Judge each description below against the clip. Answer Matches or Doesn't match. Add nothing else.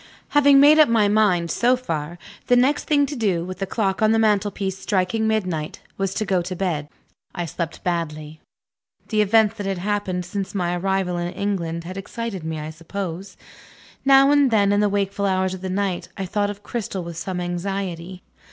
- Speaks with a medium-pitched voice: Doesn't match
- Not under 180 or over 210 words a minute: Matches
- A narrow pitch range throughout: Doesn't match